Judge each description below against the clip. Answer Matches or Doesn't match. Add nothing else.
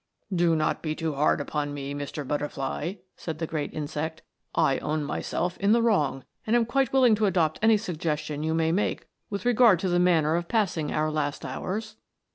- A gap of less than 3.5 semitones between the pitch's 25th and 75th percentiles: Doesn't match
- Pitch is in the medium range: Matches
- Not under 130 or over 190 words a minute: Doesn't match